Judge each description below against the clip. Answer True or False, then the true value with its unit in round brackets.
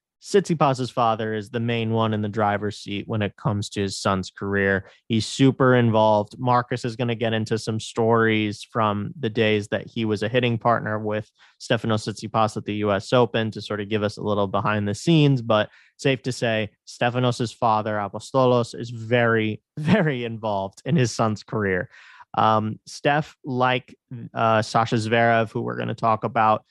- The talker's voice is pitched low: True (110 Hz)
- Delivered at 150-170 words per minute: False (180 wpm)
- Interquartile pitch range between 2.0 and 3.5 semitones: True (2.5 semitones)